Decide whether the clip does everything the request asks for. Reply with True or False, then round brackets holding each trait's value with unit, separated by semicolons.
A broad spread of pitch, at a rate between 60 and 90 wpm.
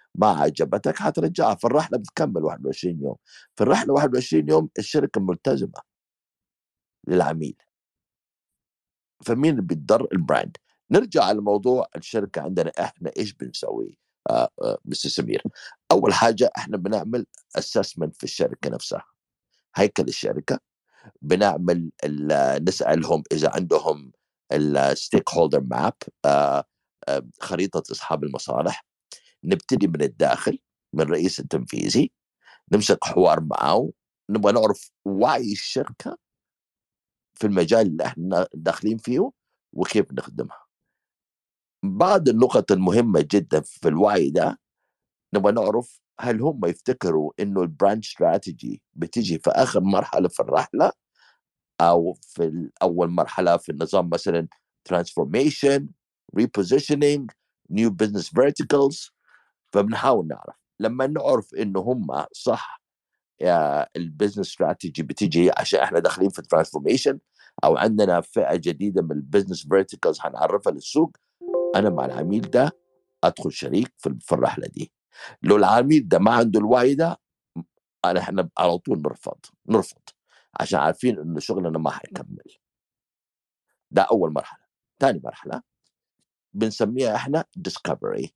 False (8.0 semitones; 110 wpm)